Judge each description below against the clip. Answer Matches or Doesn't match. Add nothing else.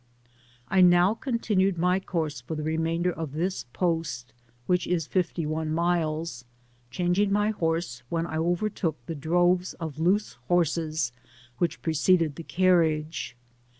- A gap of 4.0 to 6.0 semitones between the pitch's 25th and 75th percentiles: Doesn't match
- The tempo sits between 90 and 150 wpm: Matches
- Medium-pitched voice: Matches